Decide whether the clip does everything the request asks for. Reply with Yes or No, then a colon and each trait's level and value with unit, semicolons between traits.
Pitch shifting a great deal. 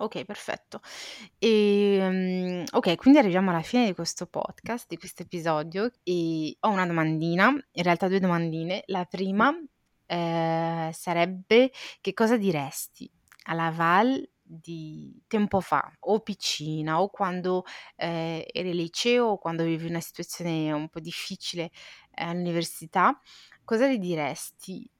No: average, 3.9 semitones